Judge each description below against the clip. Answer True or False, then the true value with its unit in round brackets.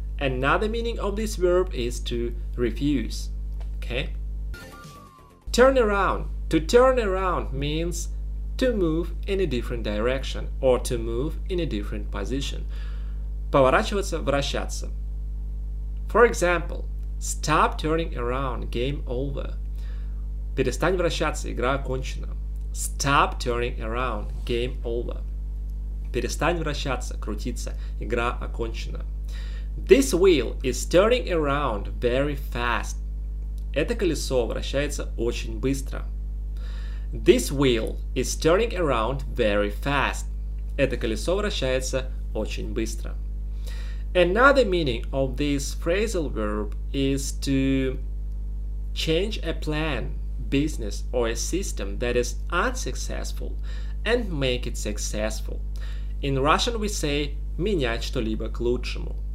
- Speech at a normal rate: False (100 wpm)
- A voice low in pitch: True (130 Hz)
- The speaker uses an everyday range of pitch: False (6.0 semitones)